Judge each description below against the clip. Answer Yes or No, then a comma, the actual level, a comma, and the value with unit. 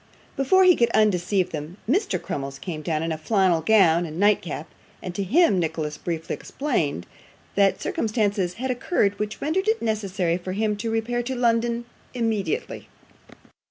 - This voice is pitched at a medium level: No, high, 205 Hz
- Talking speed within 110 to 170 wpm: Yes, average, 160 wpm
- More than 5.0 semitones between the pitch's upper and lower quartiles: Yes, wide, 5.5 semitones